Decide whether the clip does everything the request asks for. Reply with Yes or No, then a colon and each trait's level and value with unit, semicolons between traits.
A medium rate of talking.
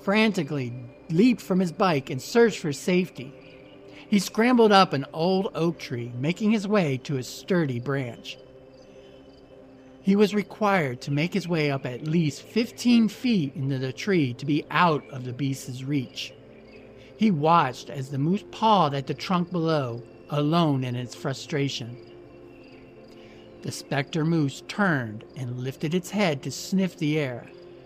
Yes: average, 155 wpm